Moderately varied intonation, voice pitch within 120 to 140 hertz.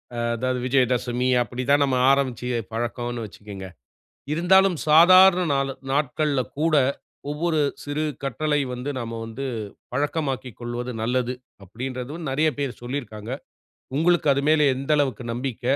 Yes: average, 3.6 semitones; low, 135 Hz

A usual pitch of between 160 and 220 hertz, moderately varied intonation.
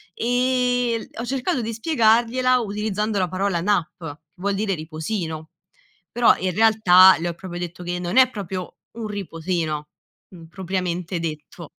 Yes: high, 190 Hz; average, 4.7 semitones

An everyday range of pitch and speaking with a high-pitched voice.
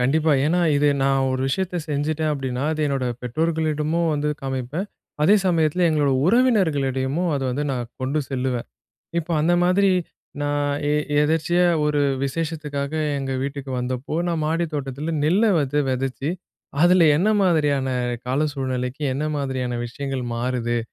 No: average, 3.5 semitones; medium, 145 Hz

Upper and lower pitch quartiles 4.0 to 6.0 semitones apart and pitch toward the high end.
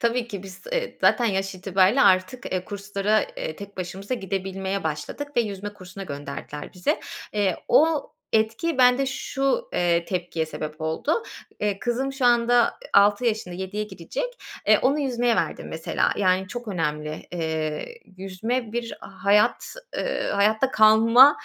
Yes: average, 4.6 semitones; high, 205 Hz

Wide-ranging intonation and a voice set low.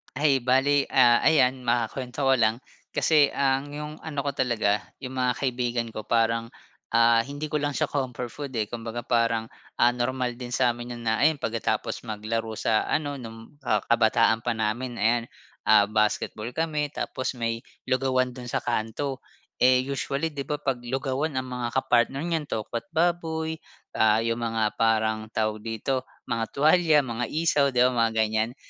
No: average, 3.3 semitones; low, 125 Hz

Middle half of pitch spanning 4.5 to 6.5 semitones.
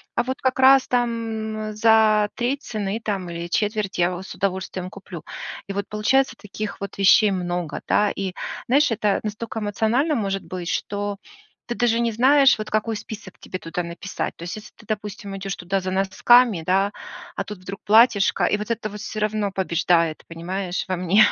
No: average, 2.9 semitones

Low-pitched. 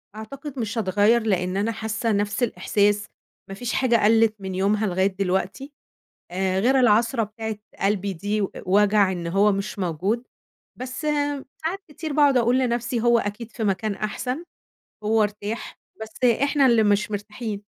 No: high, 215 Hz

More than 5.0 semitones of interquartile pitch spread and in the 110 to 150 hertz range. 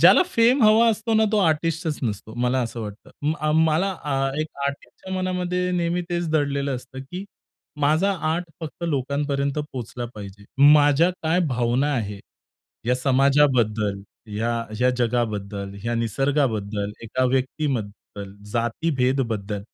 Yes: wide, 5.5 semitones; low, 135 Hz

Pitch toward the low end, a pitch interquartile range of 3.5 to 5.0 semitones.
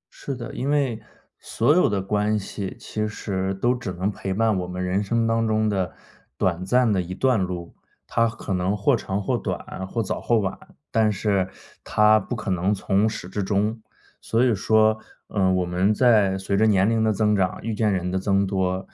No: low, 105 Hz; average, 2.8 semitones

